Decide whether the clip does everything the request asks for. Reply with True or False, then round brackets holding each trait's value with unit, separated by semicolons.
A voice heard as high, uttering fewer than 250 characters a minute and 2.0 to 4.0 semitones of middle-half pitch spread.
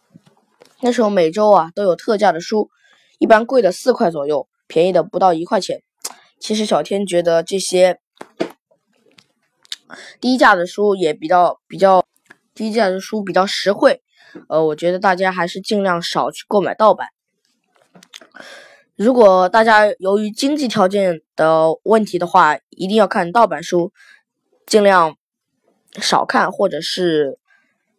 True (195 Hz; 210 characters per minute; 3.6 semitones)